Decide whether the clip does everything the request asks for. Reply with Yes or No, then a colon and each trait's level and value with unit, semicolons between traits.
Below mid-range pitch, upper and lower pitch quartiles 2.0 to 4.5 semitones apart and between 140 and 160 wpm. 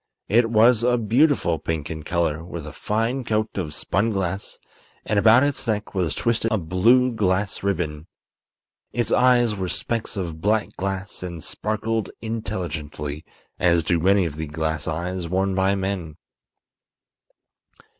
No: very low, 95 Hz; average, 4.9 semitones; average, 145 wpm